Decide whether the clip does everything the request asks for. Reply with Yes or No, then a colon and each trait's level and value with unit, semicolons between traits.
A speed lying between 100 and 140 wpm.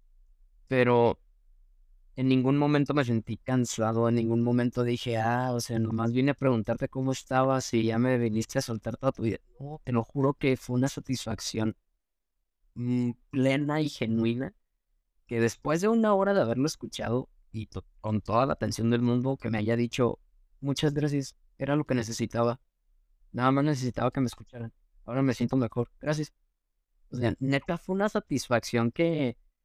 No: average, 170 wpm